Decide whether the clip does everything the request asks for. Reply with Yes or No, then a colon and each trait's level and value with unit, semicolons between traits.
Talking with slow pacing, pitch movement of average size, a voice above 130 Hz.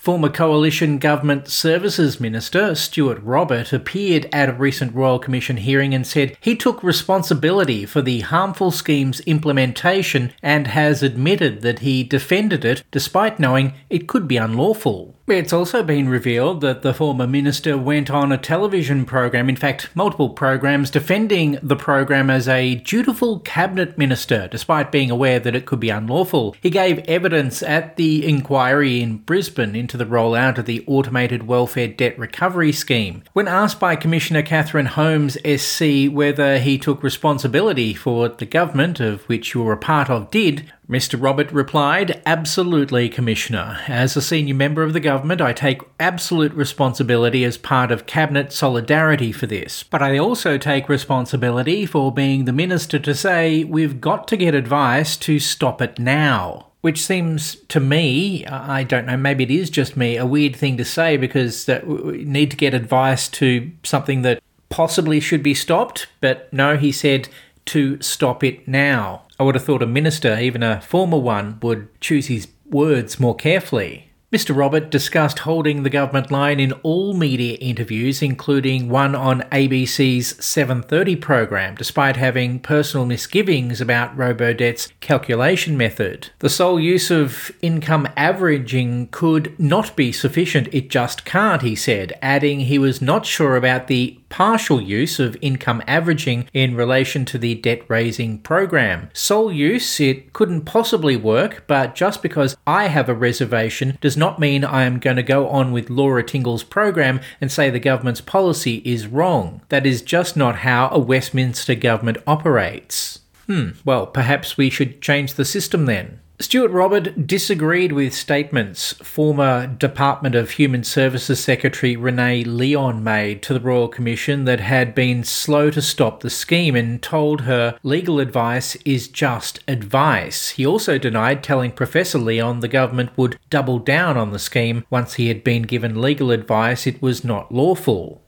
No: average, 165 wpm; average, 3.6 semitones; medium, 140 Hz